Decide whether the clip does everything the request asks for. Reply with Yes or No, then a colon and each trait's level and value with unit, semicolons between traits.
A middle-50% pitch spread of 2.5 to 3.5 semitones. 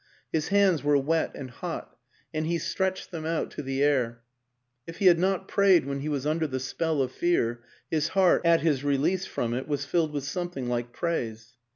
No: average, 4.3 semitones